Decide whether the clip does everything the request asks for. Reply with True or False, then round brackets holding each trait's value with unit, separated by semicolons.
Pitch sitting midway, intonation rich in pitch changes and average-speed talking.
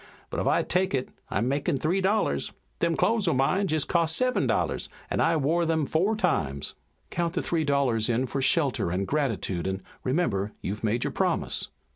True (145 Hz; 6.8 semitones; 190 wpm)